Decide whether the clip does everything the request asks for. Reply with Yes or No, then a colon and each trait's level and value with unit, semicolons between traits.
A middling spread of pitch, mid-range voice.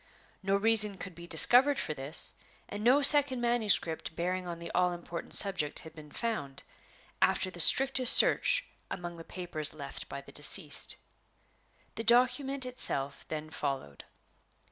No: wide, 7.4 semitones; medium, 180 Hz